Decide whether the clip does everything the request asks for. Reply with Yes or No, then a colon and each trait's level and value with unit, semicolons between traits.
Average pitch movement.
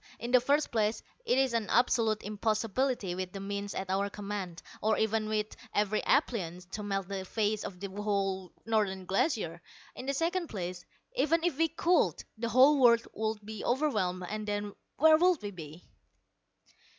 Yes: average, 4.2 semitones